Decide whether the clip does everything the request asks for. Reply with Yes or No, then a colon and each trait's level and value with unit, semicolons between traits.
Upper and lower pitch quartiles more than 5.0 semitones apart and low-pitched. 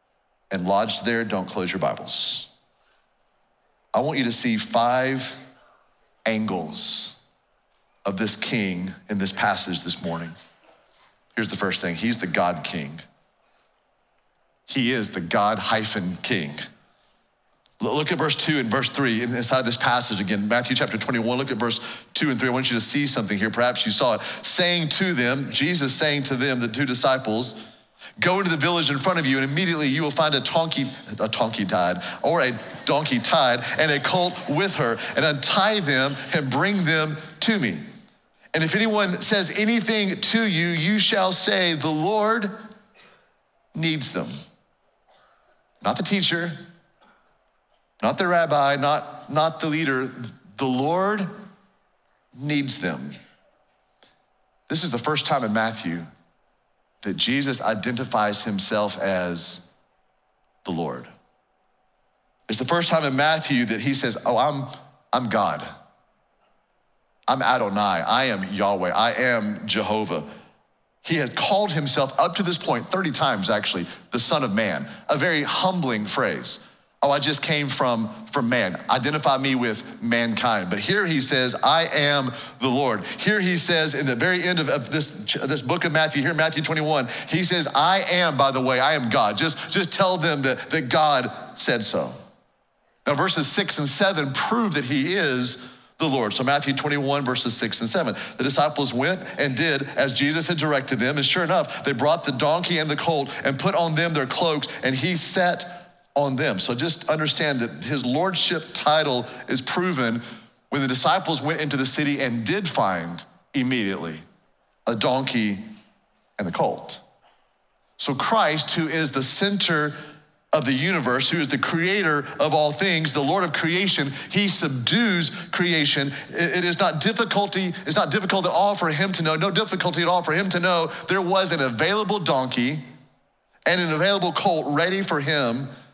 No: wide, 5.5 semitones; medium, 150 Hz